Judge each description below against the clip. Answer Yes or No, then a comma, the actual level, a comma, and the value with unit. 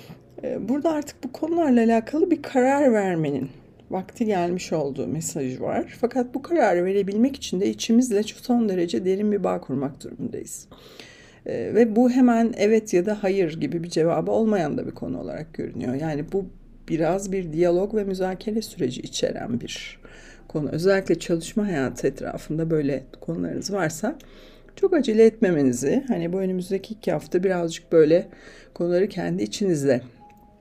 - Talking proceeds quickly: Yes, fast, 145 wpm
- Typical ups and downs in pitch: No, wide, 5.7 semitones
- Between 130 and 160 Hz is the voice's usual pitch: No, high, 190 Hz